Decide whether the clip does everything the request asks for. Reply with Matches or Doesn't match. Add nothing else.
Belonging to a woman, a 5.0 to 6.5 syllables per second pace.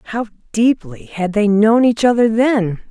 Doesn't match